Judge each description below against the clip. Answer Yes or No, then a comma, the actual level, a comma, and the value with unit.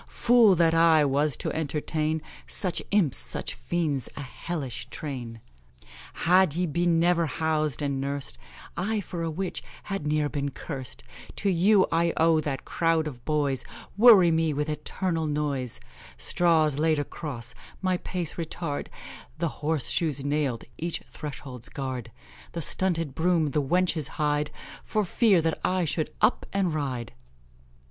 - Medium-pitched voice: Yes, medium, 155 Hz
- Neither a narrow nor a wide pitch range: Yes, average, 3.3 semitones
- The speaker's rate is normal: Yes, average, 145 wpm